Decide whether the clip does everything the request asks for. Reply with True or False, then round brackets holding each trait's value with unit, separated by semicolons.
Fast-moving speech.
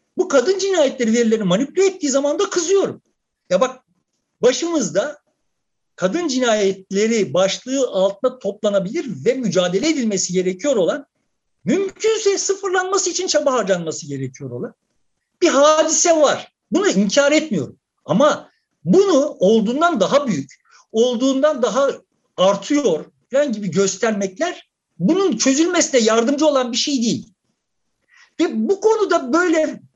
False (115 wpm)